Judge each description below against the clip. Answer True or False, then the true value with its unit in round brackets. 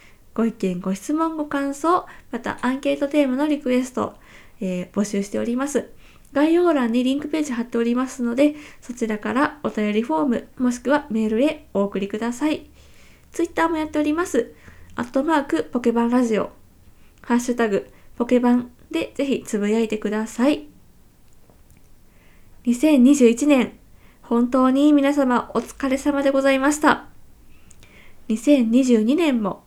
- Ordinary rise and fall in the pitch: True (4.1 semitones)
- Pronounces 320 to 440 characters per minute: False (300 characters per minute)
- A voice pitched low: False (250 Hz)